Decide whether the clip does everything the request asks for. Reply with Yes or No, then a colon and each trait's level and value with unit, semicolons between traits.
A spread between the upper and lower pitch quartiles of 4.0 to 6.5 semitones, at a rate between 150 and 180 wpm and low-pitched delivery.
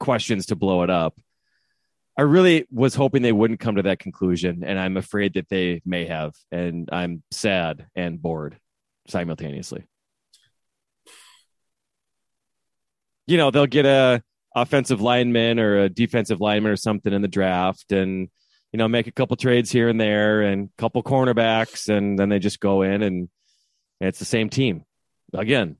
Yes: average, 4.3 semitones; average, 165 wpm; low, 105 Hz